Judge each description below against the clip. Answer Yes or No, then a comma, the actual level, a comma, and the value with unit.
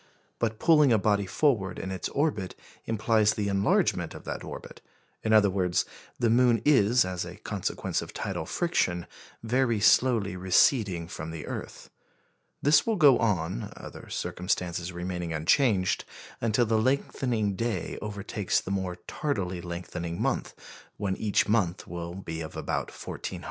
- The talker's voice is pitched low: Yes, low, 100 Hz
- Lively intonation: No, average, 4.5 semitones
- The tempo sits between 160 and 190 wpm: No, average, 150 wpm